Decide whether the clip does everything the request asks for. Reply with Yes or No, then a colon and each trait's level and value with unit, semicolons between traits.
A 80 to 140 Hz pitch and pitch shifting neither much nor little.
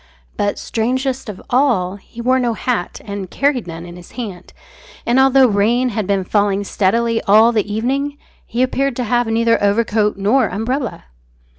No: high, 225 Hz; average, 3.7 semitones